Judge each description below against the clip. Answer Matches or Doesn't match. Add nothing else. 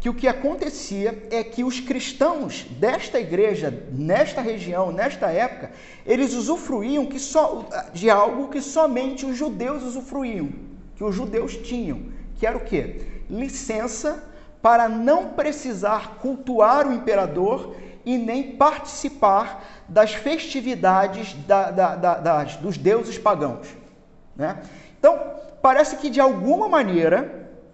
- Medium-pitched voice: Doesn't match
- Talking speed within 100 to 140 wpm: Matches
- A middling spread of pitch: Matches